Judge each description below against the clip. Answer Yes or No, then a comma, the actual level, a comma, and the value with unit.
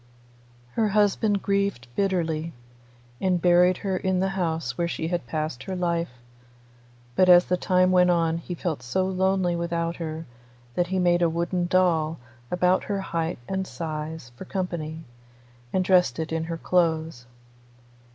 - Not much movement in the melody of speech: Yes, narrow, 2.3 semitones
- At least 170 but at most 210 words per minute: No, average, 155 wpm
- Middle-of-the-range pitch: Yes, medium, 175 Hz